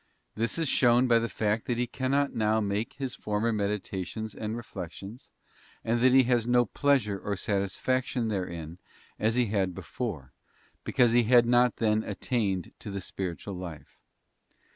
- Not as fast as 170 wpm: Yes, average, 160 wpm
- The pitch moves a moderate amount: Yes, average, 3.5 semitones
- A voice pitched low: Yes, low, 110 Hz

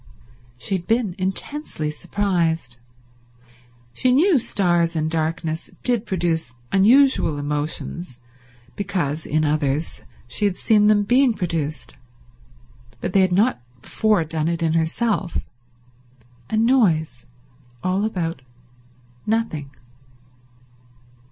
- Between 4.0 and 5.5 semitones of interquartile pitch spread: Yes, average, 5.1 semitones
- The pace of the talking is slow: Yes, slow, 105 wpm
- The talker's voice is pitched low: No, medium, 175 Hz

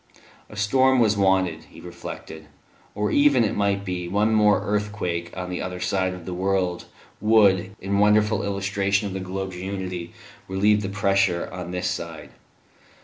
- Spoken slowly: No, average, 160 wpm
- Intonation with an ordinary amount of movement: No, narrow, 2.3 semitones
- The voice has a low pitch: Yes, very low, 95 Hz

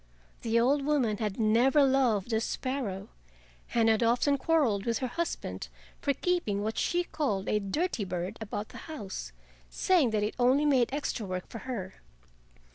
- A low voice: No, high, 235 Hz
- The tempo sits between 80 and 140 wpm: No, average, 165 wpm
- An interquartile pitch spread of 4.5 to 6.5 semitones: Yes, average, 5.0 semitones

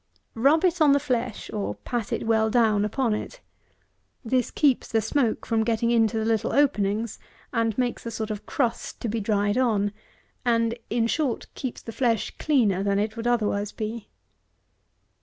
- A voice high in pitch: Yes, high, 230 Hz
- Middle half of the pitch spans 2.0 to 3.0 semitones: Yes, narrow, 2.4 semitones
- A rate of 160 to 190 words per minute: Yes, average, 175 wpm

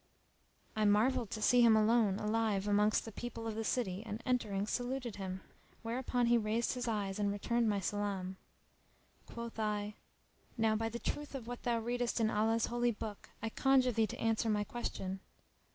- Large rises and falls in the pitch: No, narrow, 2.4 semitones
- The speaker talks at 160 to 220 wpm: Yes, average, 180 wpm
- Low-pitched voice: No, high, 225 Hz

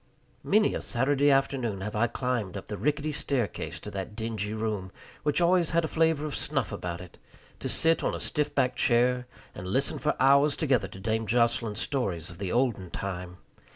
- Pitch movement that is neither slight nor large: No, wide, 5.8 semitones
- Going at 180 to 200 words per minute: Yes, average, 190 wpm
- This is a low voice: Yes, low, 120 Hz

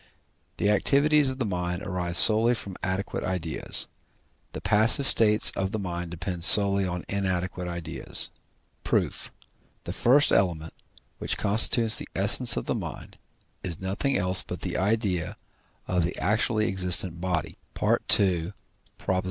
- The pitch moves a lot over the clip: No, average, 3.3 semitones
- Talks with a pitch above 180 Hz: No, very low, 95 Hz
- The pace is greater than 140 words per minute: No, slow, 135 wpm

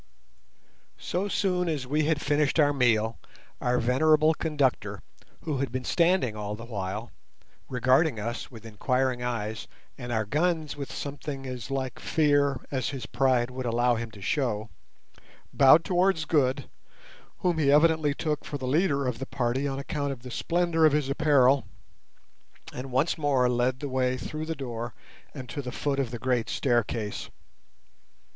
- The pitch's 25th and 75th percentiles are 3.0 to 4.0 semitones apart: Yes, average, 3.6 semitones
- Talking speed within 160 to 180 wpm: Yes, average, 165 wpm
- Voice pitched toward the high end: No, low, 135 Hz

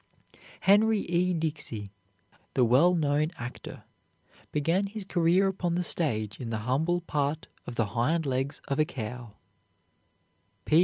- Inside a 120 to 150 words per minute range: Yes, slow, 135 wpm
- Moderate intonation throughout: No, wide, 6.0 semitones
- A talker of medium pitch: Yes, medium, 150 Hz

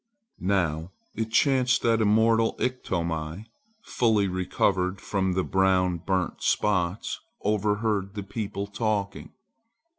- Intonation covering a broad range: No, average, 3.0 semitones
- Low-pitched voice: Yes, low, 100 Hz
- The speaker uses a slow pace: Yes, slow, 100 wpm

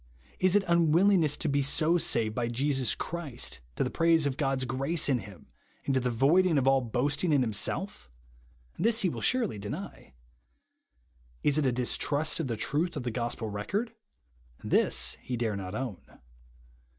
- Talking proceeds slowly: No, average, 175 wpm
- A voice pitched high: No, medium, 140 Hz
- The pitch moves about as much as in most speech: No, wide, 5.7 semitones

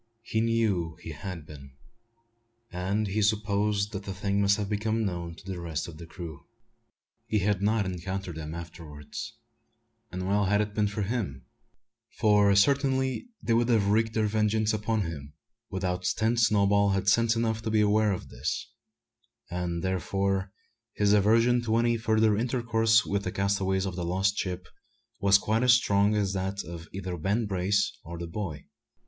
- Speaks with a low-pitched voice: Yes, low, 100 Hz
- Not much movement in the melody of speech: No, average, 3.2 semitones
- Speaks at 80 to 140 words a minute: No, average, 170 wpm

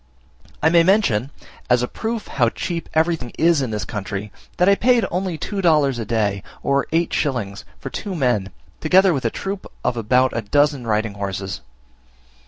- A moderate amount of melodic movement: No, wide, 7.7 semitones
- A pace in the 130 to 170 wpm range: No, average, 180 wpm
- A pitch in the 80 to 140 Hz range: Yes, low, 135 Hz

